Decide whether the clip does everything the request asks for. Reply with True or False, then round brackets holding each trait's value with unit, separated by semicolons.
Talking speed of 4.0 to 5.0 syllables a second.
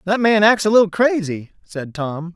True (4.8 syllables/s)